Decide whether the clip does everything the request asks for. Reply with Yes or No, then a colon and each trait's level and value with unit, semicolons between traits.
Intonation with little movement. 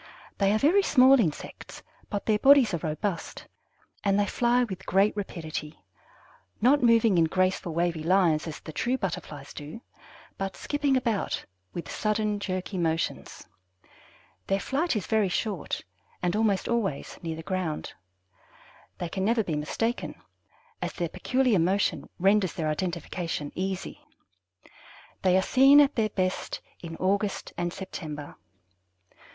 No: average, 4.7 semitones